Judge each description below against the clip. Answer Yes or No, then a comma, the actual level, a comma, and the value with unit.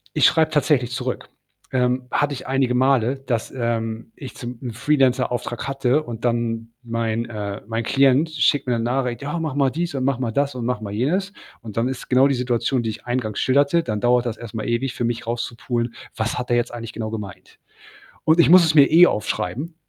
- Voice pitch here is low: Yes, low, 125 Hz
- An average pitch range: Yes, average, 3.0 semitones